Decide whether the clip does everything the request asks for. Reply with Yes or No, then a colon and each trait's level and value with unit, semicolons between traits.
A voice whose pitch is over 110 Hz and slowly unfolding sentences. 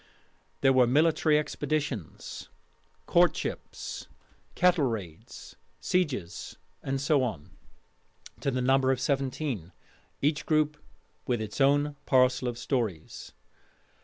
Yes: low, 135 Hz; slow, 105 wpm